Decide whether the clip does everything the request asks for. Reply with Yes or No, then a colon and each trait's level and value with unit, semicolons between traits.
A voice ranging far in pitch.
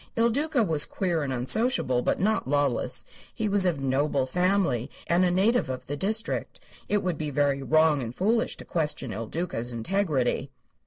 Yes: wide, 6.8 semitones